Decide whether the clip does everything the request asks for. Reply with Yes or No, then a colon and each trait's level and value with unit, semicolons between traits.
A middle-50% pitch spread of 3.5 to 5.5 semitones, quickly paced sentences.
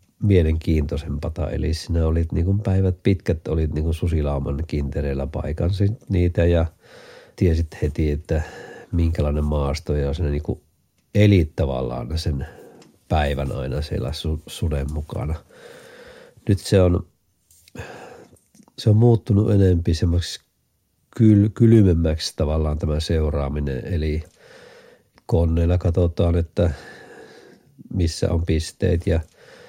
No: average, 3.8 semitones; average, 105 wpm